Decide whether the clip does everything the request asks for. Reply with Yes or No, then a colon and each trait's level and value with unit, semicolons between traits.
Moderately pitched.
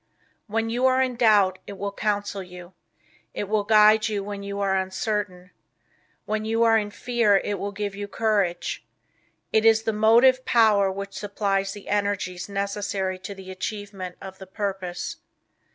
No: high, 205 Hz